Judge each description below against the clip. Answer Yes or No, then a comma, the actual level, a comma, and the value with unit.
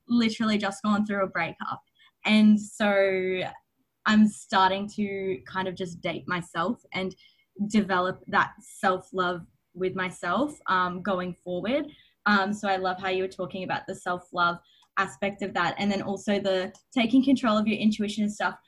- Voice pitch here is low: No, high, 195 Hz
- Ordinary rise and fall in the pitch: No, narrow, 2.3 semitones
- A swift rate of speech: No, average, 165 wpm